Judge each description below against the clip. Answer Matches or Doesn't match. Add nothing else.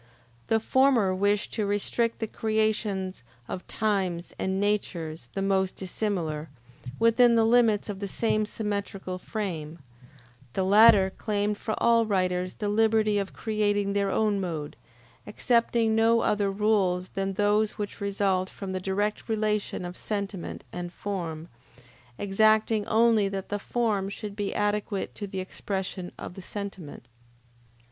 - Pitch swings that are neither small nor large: Doesn't match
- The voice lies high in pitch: Matches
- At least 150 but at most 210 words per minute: Doesn't match